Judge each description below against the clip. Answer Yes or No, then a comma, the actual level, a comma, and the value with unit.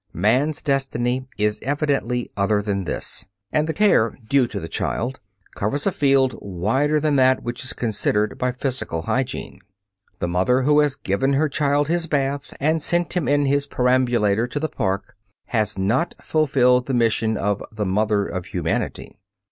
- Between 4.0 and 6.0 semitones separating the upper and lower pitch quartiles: Yes, average, 5.1 semitones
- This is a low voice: Yes, low, 130 Hz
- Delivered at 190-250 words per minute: No, average, 165 wpm